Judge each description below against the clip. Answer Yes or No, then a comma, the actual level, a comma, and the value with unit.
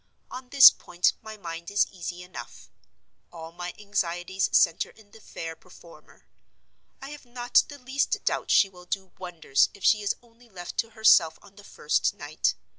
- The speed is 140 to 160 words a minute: No, average, 175 wpm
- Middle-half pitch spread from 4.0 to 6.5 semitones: Yes, average, 4.3 semitones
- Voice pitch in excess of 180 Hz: Yes, high, 190 Hz